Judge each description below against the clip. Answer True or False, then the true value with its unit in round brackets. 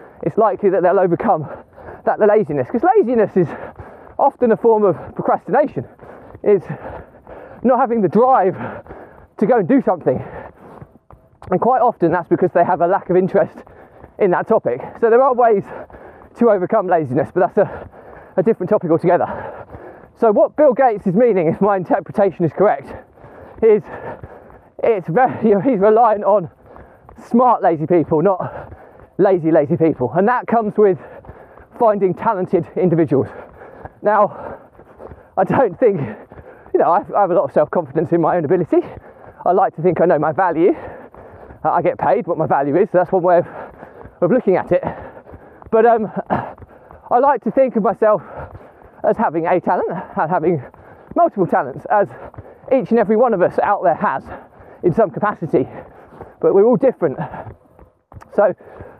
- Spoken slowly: False (170 wpm)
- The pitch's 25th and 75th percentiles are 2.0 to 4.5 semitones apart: False (5.1 semitones)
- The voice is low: False (205 Hz)